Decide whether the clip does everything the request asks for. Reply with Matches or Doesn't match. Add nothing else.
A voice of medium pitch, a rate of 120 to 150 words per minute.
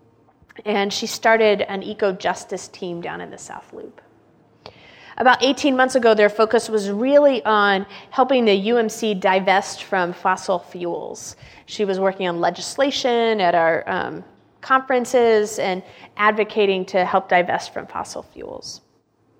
Doesn't match